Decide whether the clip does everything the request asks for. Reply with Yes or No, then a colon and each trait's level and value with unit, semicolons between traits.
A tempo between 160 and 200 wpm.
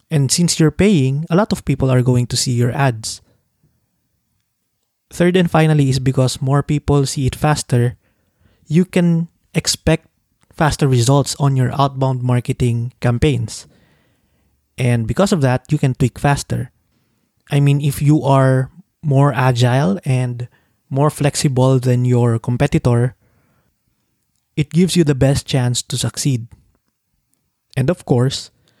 No: average, 140 wpm